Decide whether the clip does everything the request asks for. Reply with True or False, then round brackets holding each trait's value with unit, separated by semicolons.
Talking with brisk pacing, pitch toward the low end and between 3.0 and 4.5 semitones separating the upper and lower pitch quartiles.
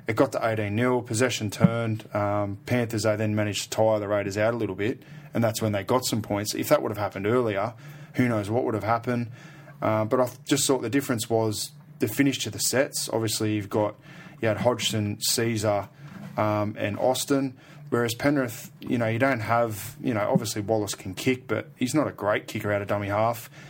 True (215 wpm; 115 Hz; 3.5 semitones)